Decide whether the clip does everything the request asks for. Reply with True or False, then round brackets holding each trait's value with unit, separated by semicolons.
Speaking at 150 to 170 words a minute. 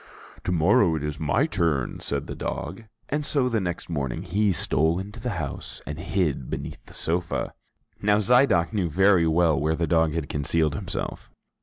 False (185 wpm)